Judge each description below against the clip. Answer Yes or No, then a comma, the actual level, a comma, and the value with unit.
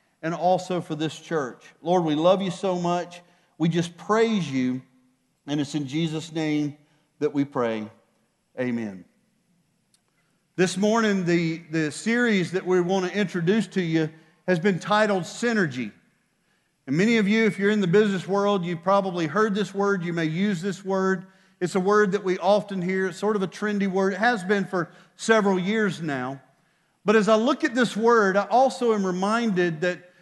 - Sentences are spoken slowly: No, average, 185 wpm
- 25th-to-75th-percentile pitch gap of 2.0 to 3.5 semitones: No, average, 3.9 semitones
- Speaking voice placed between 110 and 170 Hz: No, medium, 185 Hz